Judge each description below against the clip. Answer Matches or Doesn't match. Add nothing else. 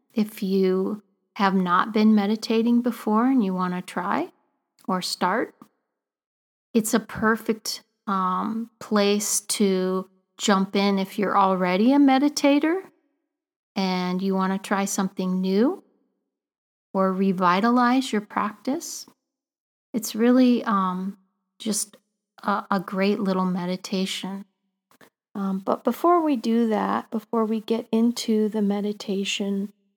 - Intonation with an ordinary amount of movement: Matches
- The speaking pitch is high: Matches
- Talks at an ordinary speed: Doesn't match